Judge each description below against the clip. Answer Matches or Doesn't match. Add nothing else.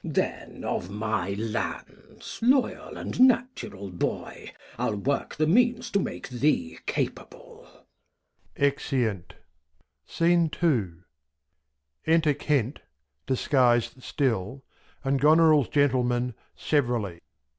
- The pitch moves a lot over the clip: Matches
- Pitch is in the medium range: Doesn't match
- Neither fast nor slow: Doesn't match